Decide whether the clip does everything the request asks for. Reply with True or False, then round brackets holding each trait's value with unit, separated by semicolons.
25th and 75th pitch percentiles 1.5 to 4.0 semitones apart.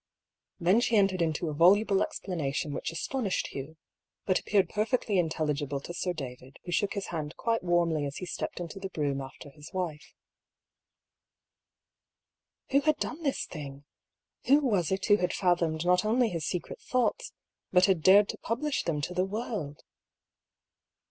False (4.9 semitones)